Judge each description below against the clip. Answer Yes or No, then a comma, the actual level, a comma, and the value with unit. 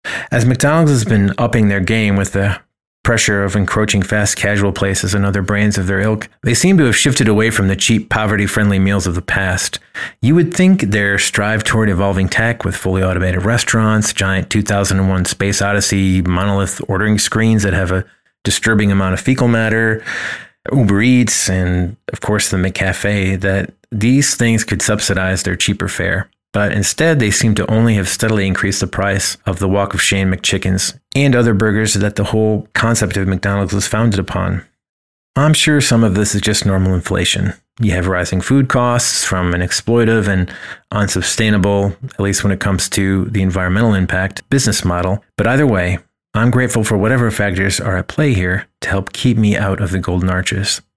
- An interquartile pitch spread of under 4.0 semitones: Yes, narrow, 2.6 semitones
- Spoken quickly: No, average, 185 wpm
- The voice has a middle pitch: No, low, 100 Hz